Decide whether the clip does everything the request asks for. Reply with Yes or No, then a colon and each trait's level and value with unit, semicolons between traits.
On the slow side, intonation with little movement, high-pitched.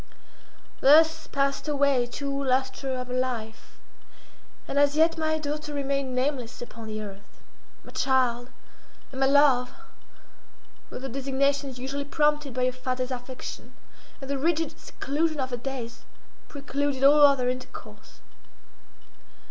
Yes: slow, 130 wpm; narrow, 2.2 semitones; very high, 270 Hz